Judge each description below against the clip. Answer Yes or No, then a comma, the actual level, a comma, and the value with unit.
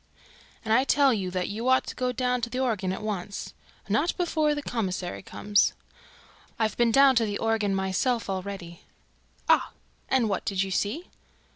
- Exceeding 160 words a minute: Yes, average, 175 wpm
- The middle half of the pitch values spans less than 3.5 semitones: No, average, 4.7 semitones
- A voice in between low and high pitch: No, high, 220 Hz